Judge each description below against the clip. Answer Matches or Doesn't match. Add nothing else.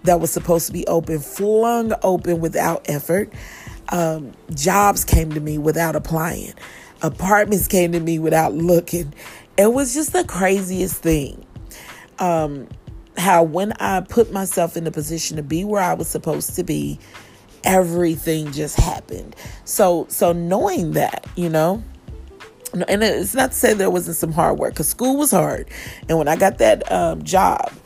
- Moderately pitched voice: Matches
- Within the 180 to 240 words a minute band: Doesn't match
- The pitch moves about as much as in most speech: Matches